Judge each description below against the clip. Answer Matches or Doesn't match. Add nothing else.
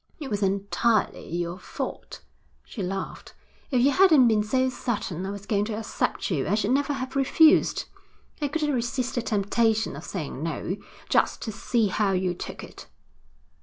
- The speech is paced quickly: Doesn't match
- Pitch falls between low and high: Doesn't match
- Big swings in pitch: Doesn't match